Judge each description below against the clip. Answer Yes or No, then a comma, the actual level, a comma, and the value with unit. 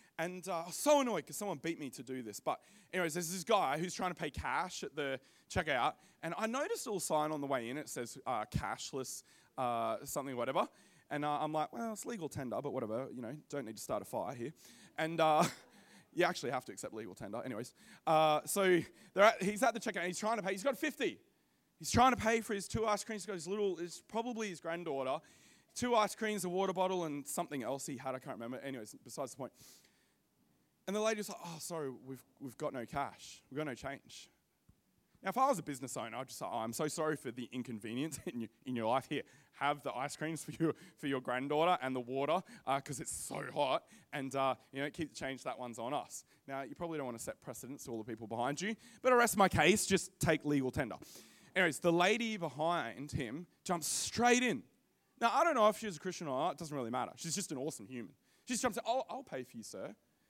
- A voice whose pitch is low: No, medium, 160 Hz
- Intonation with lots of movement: Yes, wide, 6.4 semitones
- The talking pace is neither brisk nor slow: No, fast, 250 wpm